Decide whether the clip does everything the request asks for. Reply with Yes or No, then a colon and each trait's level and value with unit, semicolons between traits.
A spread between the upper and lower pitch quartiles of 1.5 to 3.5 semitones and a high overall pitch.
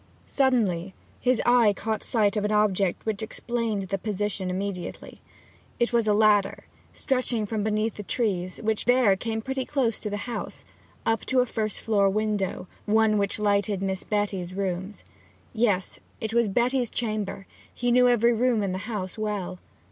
Yes: average, 2.8 semitones; high, 215 Hz